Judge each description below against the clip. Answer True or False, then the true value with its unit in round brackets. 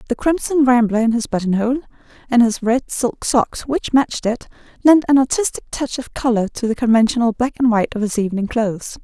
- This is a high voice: True (240 Hz)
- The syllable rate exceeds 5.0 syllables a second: True (5.7 syllables/s)